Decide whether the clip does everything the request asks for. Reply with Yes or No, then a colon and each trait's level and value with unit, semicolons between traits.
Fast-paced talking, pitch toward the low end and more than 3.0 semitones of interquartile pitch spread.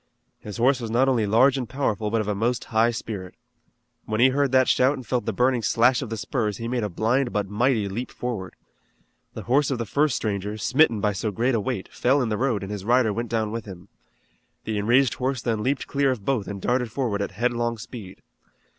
Yes: fast, 230 wpm; low, 115 Hz; average, 3.4 semitones